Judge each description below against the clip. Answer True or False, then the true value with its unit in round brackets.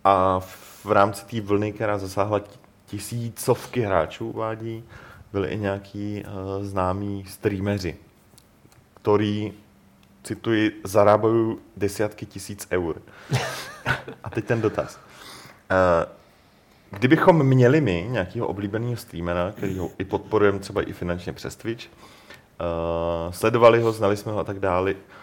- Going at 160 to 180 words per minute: False (120 wpm)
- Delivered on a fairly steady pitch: True (2.3 semitones)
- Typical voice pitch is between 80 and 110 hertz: True (100 Hz)